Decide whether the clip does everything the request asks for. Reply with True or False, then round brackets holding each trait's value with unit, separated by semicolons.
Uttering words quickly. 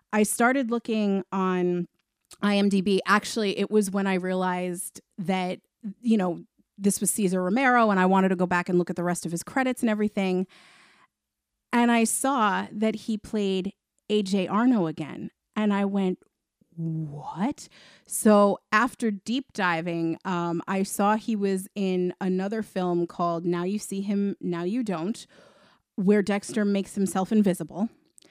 False (155 wpm)